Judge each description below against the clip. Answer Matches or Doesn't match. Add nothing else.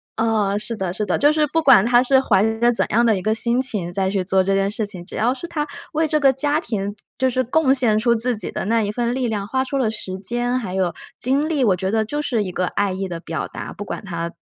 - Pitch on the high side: Matches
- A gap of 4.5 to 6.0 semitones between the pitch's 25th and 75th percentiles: Matches